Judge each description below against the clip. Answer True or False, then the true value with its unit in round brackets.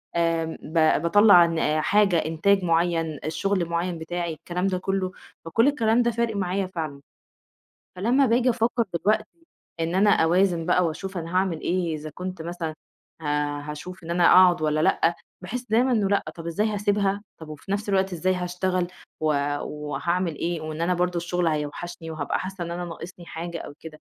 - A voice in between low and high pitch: True (175 Hz)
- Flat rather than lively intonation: False (3.0 semitones)